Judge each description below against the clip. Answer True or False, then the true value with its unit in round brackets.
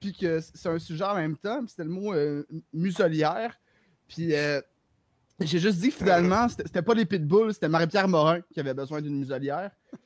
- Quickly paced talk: False (195 wpm)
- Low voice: False (165 Hz)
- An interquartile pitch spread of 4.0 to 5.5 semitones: True (4.7 semitones)